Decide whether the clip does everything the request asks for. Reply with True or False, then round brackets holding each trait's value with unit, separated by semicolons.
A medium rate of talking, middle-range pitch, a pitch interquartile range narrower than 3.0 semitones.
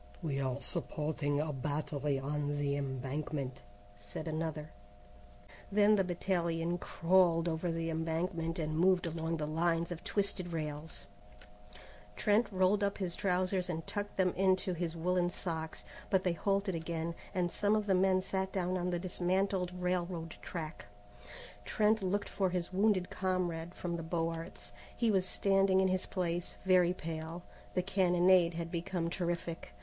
True (155 wpm; 175 Hz; 2.5 semitones)